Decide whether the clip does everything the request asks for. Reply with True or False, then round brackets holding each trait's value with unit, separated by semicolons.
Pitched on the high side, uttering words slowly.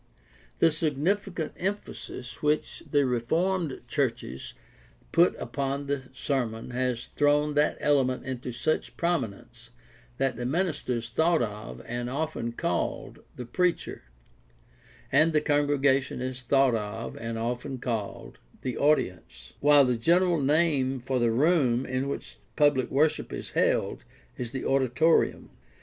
False (135 Hz; 130 wpm)